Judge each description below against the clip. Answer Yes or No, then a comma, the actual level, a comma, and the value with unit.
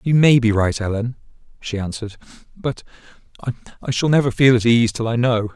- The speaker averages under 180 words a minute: No, average, 185 wpm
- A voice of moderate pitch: No, low, 120 Hz